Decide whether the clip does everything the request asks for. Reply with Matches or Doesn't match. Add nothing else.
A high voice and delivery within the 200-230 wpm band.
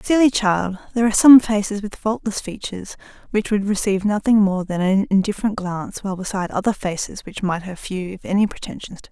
Matches